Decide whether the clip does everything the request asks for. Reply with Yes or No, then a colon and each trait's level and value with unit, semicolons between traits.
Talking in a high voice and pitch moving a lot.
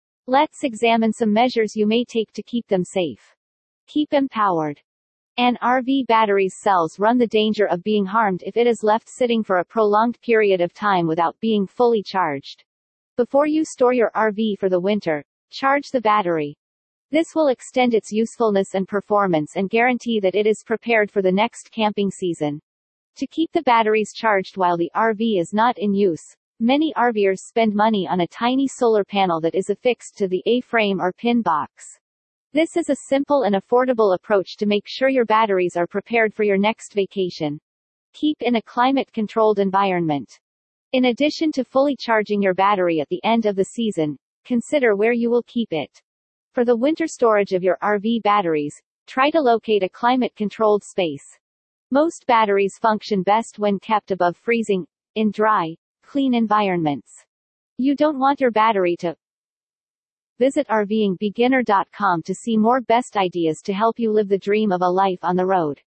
No: high, 215 Hz; average, 3.8 semitones